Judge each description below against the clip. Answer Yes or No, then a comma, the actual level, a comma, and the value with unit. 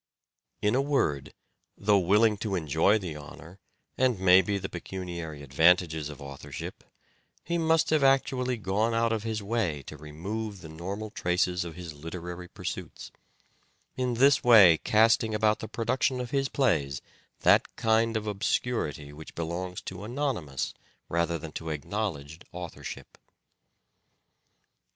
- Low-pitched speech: Yes, very low, 95 Hz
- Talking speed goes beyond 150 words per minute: No, slow, 135 wpm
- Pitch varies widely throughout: Yes, wide, 5.7 semitones